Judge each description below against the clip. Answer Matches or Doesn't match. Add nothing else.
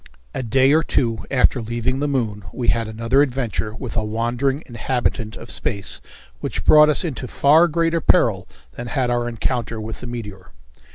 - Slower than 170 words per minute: Doesn't match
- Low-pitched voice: Matches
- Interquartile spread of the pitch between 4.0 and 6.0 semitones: Doesn't match